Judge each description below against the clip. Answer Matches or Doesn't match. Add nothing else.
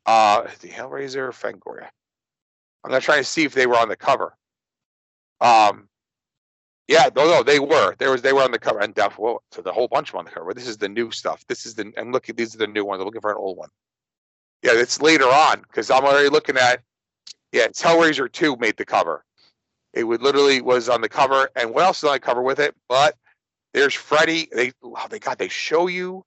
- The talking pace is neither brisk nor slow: Doesn't match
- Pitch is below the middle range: Matches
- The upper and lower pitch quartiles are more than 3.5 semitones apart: Matches